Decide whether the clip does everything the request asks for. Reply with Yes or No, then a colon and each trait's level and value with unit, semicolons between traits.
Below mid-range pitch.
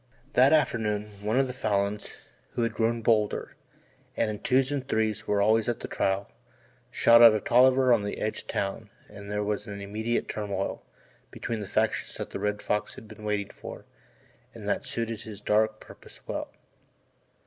Yes: low, 110 Hz